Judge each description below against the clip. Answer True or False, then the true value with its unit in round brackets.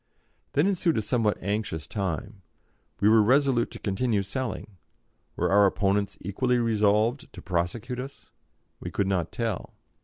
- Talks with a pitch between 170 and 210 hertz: False (105 Hz)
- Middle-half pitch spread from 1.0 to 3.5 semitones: False (3.9 semitones)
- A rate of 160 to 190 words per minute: False (145 wpm)